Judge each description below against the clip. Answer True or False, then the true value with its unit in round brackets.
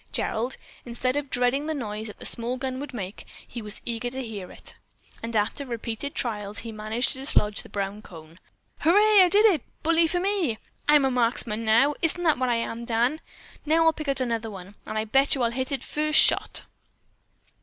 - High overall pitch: True (245 Hz)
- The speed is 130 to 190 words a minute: False (205 wpm)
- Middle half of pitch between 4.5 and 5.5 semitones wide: True (4.9 semitones)